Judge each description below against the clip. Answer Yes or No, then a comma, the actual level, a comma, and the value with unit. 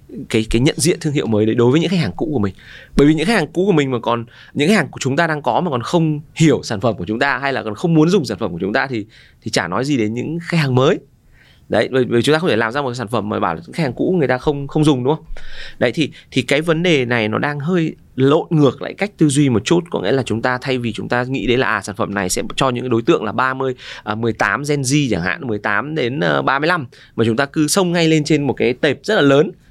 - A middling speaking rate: No, fast, 310 wpm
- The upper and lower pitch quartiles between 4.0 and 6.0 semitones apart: Yes, average, 4.9 semitones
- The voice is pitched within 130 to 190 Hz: Yes, low, 135 Hz